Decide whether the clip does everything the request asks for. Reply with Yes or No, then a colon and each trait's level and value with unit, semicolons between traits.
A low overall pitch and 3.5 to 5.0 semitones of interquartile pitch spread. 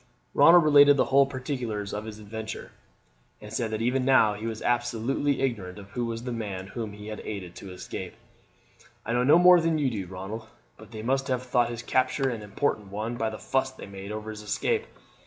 Yes: low, 115 Hz; average, 3.9 semitones